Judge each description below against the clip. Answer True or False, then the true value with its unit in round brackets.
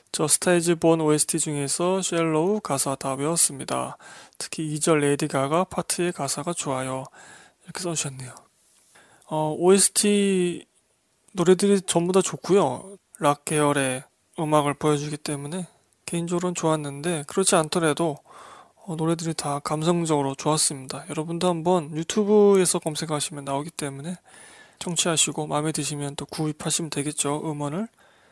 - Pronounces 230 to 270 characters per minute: False (325 characters per minute)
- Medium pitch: True (160 Hz)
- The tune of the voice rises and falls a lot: False (3.4 semitones)